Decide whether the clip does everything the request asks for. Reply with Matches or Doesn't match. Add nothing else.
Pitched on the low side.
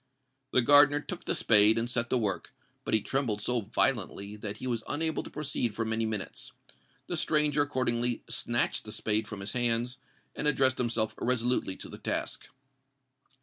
Matches